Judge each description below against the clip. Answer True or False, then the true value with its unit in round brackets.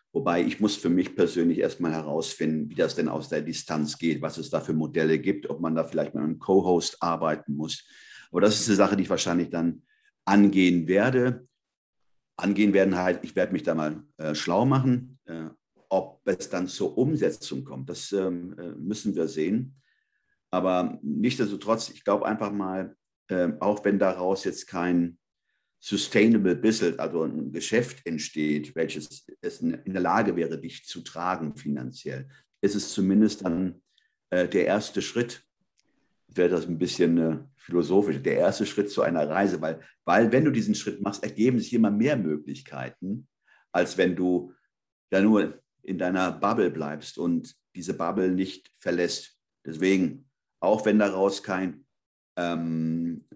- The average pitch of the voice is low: True (90 Hz)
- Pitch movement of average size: True (3.9 semitones)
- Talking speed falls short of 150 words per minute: False (160 wpm)